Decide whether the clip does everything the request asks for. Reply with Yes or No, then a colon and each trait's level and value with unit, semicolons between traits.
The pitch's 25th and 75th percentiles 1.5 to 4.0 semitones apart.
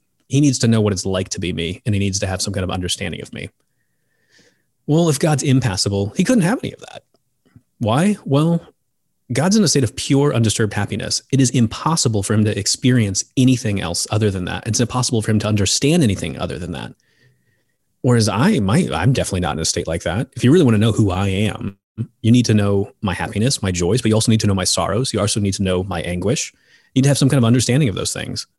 No: average, 4.6 semitones